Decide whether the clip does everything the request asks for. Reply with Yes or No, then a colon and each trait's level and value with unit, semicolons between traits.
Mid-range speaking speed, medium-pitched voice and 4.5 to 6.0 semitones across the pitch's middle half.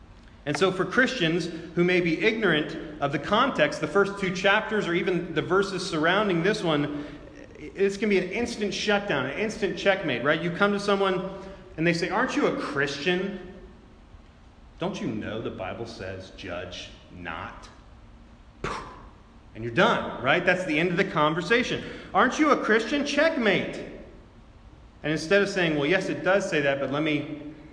Yes: average, 170 wpm; medium, 175 Hz; average, 5.1 semitones